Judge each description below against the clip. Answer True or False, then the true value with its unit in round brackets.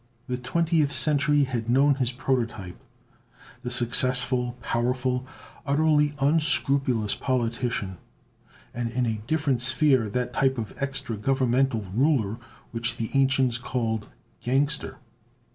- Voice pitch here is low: True (125 Hz)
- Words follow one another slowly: True (110 wpm)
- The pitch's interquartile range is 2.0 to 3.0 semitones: True (2.7 semitones)